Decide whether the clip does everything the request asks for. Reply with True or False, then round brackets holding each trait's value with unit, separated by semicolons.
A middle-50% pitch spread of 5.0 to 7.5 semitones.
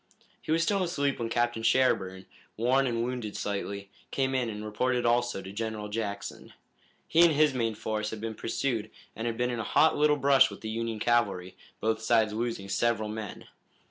False (3.0 semitones)